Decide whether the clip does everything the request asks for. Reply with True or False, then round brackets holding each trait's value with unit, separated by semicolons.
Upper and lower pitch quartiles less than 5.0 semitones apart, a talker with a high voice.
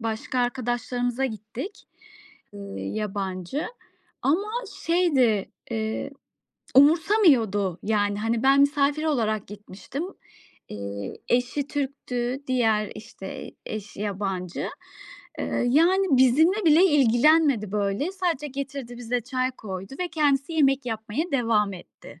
False (5.3 semitones; 245 Hz)